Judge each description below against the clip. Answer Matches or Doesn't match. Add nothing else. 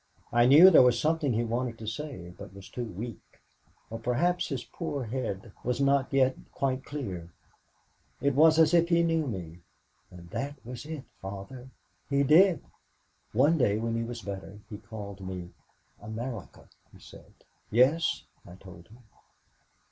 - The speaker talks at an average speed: Matches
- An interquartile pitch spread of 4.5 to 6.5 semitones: Matches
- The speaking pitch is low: Matches